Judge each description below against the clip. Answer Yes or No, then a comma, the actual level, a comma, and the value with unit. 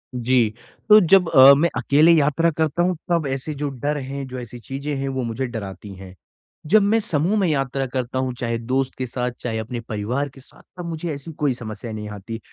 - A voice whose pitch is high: No, low, 135 Hz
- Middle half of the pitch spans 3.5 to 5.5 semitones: Yes, average, 4.0 semitones